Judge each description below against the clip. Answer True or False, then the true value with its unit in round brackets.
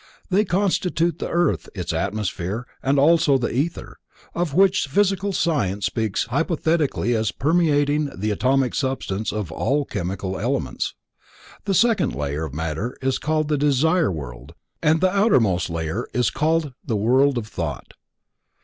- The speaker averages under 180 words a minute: True (145 wpm)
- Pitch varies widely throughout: True (8.3 semitones)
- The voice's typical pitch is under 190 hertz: True (135 Hz)